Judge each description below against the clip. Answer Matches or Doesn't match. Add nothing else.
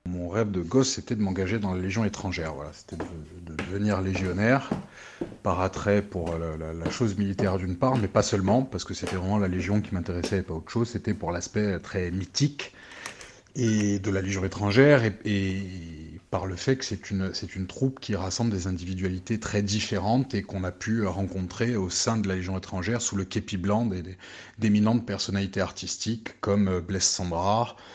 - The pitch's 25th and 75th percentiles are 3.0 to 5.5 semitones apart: Doesn't match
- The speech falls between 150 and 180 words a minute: Doesn't match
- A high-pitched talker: Doesn't match